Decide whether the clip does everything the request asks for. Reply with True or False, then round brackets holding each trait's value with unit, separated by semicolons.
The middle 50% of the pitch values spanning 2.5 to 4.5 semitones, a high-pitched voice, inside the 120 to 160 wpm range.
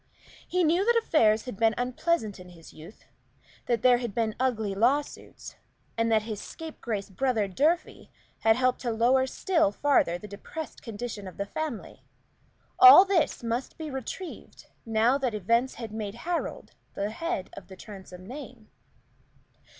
False (5.1 semitones; 235 Hz; 155 wpm)